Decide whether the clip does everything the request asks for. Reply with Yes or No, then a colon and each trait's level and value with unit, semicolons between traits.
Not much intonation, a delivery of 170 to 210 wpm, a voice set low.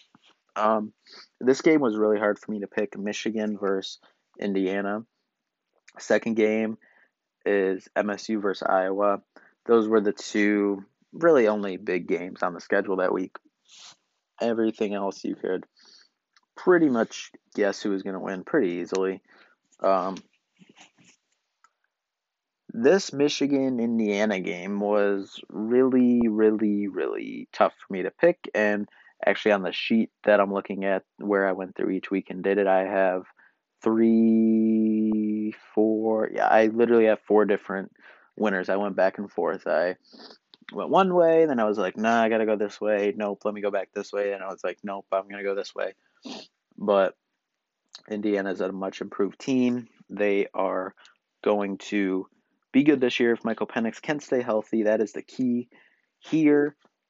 No: narrow, 2.2 semitones; average, 160 wpm; low, 105 Hz